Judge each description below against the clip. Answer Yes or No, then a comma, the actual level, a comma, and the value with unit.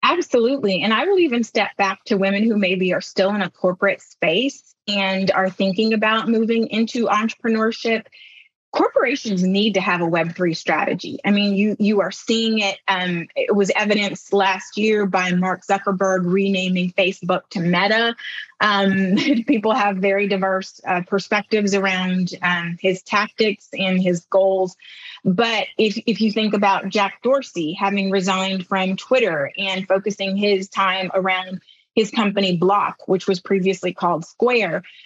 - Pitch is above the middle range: Yes, high, 195 Hz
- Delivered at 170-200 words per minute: No, average, 155 wpm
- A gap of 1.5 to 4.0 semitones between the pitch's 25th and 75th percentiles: Yes, narrow, 2.6 semitones